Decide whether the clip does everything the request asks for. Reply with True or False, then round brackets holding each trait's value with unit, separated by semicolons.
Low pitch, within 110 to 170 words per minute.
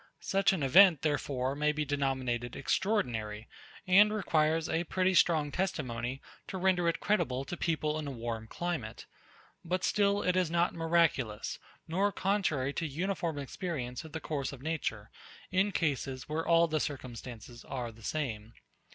False (155 Hz; 155 wpm)